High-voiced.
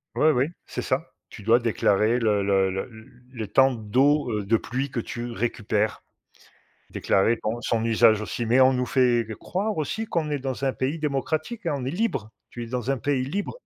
No: low, 125 Hz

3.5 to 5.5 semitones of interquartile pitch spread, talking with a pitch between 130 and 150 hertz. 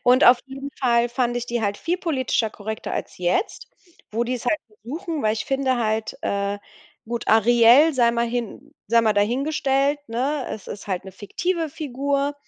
No: average, 4.0 semitones; high, 240 Hz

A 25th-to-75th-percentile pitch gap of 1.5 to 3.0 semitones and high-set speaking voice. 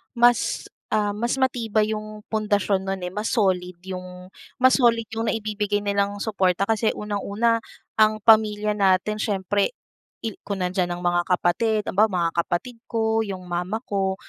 Yes: average, 2.7 semitones; high, 205 Hz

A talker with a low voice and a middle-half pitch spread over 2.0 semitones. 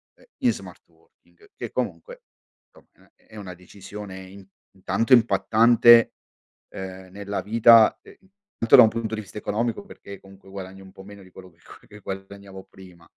Yes: low, 100 Hz; average, 2.8 semitones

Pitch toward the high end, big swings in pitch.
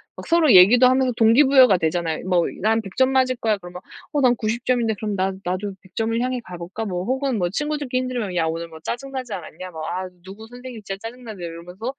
Yes: high, 220 Hz; wide, 5.8 semitones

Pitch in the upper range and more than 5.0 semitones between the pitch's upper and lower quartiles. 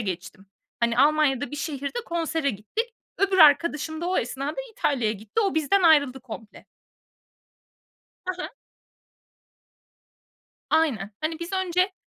Yes: very high, 300 Hz; wide, 5.6 semitones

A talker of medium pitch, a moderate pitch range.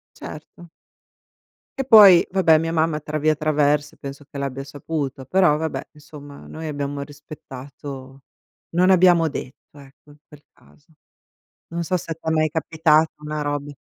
No: medium, 150 Hz; narrow, 2.3 semitones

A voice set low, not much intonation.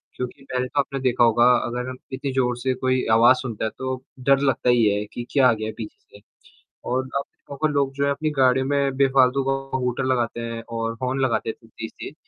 Yes: low, 130 Hz; narrow, 2.2 semitones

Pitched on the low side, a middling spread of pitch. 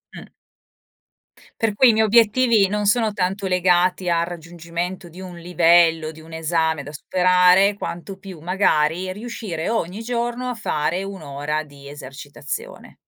No: medium, 180 Hz; average, 4.0 semitones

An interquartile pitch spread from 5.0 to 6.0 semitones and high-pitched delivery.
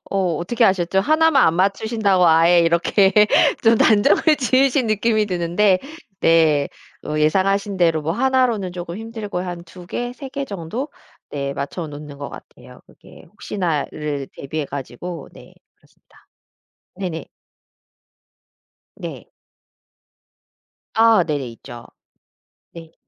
No: average, 5.3 semitones; medium, 180 Hz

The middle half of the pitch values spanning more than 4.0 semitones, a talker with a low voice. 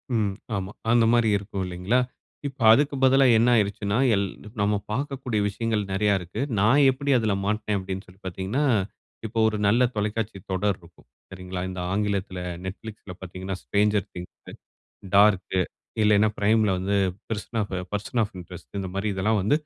No: average, 2.7 semitones; low, 105 Hz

